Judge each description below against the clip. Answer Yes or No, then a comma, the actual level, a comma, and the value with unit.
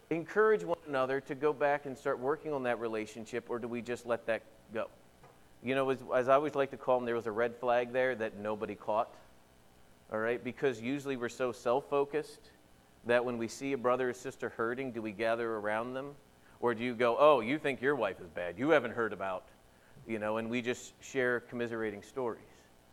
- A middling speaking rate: No, fast, 215 wpm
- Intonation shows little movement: No, average, 3.4 semitones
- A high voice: No, low, 120 Hz